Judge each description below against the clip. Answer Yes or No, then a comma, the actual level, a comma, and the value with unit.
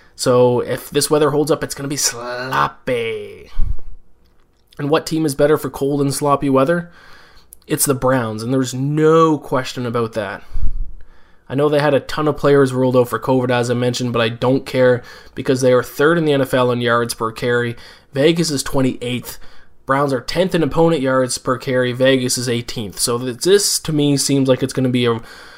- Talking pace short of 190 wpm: No, average, 200 wpm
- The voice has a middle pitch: No, low, 130 Hz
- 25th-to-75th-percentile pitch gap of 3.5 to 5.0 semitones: No, average, 3.1 semitones